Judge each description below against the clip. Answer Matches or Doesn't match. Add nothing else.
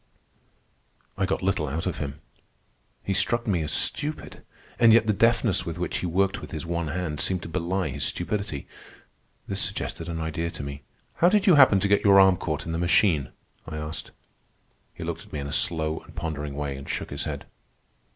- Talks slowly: Doesn't match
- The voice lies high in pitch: Doesn't match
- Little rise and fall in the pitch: Doesn't match